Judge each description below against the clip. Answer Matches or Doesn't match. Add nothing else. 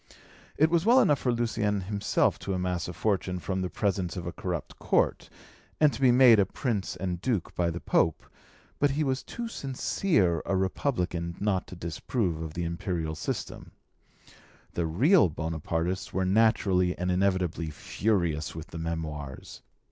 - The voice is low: Matches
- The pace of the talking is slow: Doesn't match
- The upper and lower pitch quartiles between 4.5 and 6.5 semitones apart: Matches